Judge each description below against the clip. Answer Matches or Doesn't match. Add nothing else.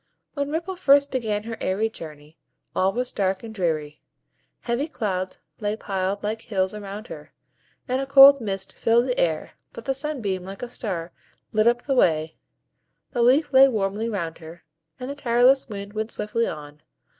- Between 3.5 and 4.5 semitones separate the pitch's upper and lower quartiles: Doesn't match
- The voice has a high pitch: Matches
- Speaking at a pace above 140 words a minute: Matches